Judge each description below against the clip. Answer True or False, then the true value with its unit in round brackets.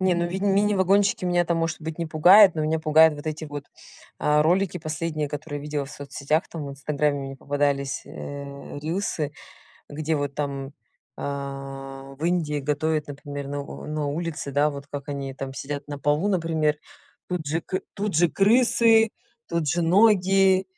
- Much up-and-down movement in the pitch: False (3.3 semitones)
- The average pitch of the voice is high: False (155 Hz)